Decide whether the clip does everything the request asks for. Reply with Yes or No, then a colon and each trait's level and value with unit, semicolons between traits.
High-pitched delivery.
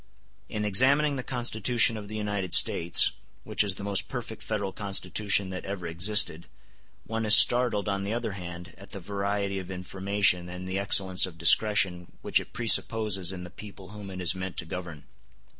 No: low, 100 Hz